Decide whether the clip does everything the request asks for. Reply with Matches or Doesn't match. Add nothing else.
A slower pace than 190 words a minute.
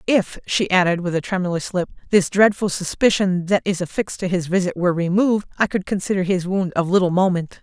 Doesn't match